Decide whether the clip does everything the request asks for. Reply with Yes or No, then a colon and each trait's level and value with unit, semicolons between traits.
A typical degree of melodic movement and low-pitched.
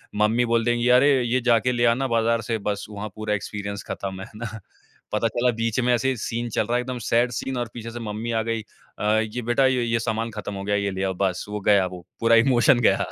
No: narrow, 2.3 semitones; low, 115 Hz